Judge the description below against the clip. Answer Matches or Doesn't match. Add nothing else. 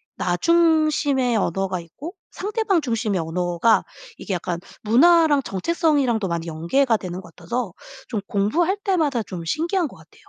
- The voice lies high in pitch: Matches